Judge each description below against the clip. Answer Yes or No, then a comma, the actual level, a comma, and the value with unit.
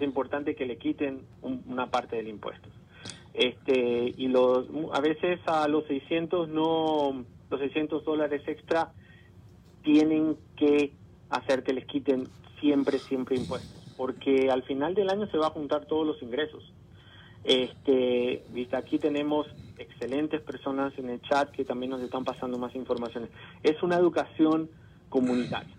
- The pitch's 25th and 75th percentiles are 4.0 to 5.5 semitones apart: No, average, 3.3 semitones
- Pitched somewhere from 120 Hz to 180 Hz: Yes, medium, 140 Hz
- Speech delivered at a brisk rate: No, average, 145 wpm